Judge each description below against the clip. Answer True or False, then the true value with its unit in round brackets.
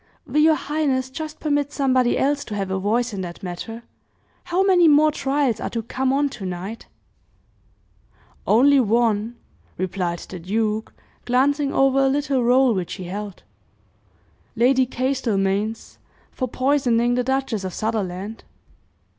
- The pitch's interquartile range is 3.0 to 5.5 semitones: True (4.9 semitones)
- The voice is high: True (245 Hz)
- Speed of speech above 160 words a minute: False (140 wpm)